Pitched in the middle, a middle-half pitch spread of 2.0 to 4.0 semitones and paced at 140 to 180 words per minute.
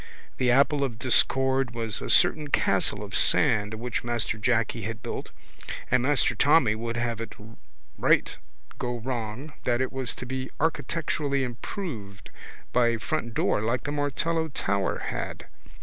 No: low, 125 Hz; average, 3.4 semitones; average, 150 wpm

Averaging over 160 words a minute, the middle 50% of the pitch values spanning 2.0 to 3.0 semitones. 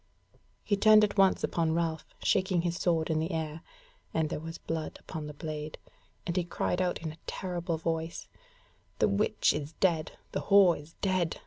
Yes: average, 180 wpm; narrow, 2.6 semitones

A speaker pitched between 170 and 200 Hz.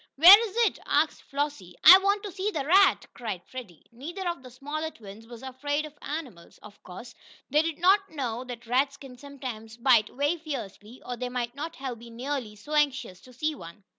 No: very high, 265 Hz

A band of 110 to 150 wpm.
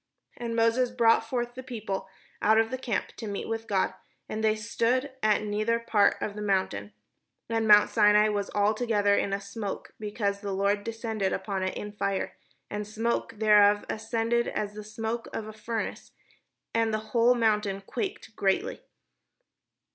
No: average, 170 wpm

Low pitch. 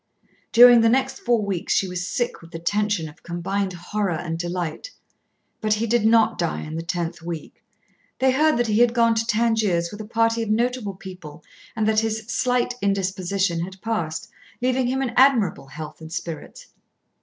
No: high, 210 Hz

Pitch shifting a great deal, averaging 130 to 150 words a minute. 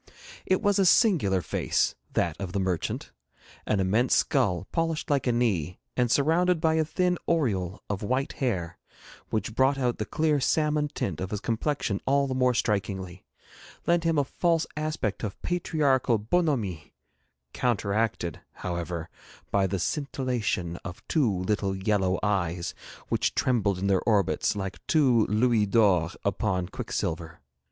Yes: wide, 7.1 semitones; average, 145 wpm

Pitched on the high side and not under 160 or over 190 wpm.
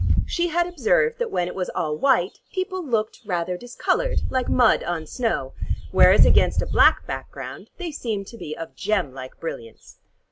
Yes: high, 225 Hz; average, 175 wpm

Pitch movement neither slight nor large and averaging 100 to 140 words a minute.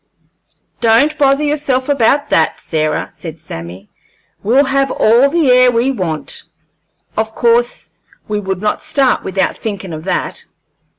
No: wide, 6.5 semitones; slow, 135 wpm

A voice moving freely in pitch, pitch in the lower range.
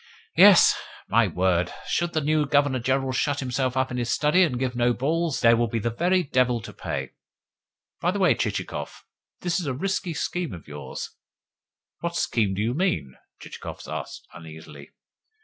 No: average, 5.0 semitones; low, 130 Hz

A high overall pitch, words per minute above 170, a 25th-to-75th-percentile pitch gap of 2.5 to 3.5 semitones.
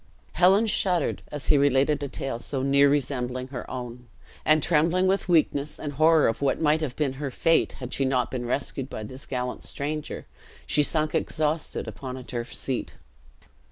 No: medium, 140 Hz; average, 180 wpm; average, 3.1 semitones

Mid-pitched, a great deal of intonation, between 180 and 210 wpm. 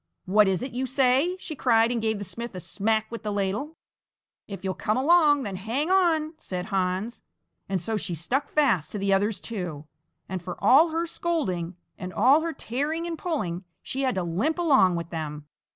No: high, 220 Hz; wide, 7.6 semitones; average, 200 wpm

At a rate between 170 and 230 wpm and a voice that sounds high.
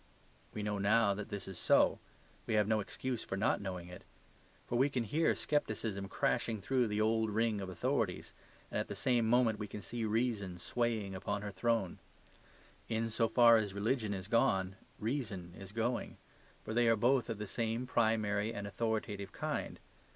No: average, 180 wpm; low, 110 Hz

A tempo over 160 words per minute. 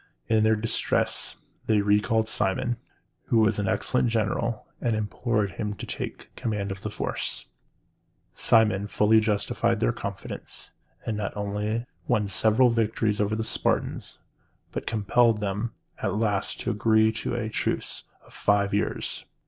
No: average, 145 wpm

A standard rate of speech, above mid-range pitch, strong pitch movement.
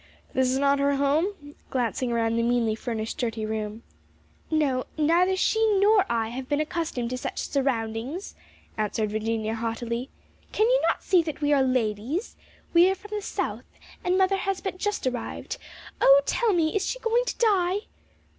Yes: average, 175 wpm; very high, 280 Hz; wide, 8.3 semitones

